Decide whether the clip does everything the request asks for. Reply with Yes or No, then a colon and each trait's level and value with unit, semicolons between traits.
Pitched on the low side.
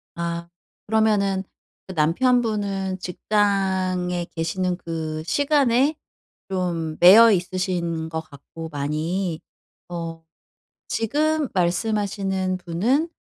No: medium, 185 Hz